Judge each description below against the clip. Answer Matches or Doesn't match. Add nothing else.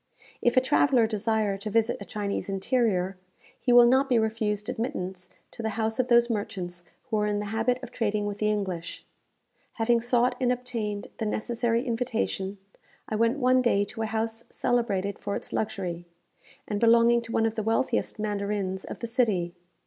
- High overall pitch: Matches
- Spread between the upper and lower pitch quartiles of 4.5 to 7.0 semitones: Doesn't match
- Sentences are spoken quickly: Doesn't match